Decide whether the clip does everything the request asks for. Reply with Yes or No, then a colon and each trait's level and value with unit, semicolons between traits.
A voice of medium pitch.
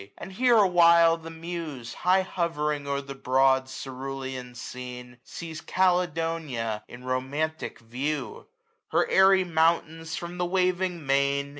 Yes: medium, 155 Hz